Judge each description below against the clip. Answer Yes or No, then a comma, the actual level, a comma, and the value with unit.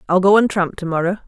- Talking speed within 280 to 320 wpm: Yes, fast, 285 wpm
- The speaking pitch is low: No, medium, 185 Hz